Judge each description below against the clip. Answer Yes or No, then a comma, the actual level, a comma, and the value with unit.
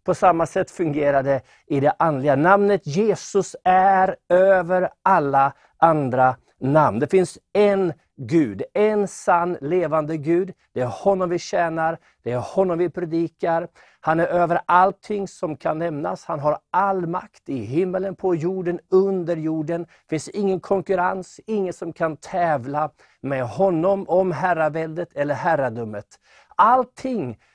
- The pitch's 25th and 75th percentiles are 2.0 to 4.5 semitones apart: Yes, average, 3.4 semitones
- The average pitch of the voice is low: No, medium, 175 Hz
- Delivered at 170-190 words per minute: No, average, 140 wpm